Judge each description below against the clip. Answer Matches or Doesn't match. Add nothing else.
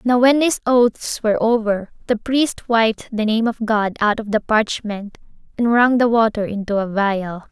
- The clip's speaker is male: Doesn't match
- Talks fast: Doesn't match